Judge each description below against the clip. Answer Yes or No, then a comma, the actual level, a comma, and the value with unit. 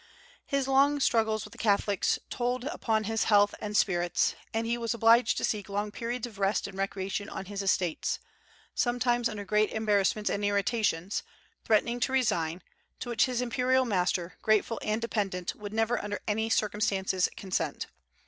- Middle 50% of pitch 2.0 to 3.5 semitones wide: Yes, average, 2.9 semitones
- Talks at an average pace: Yes, average, 165 wpm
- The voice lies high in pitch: Yes, high, 215 Hz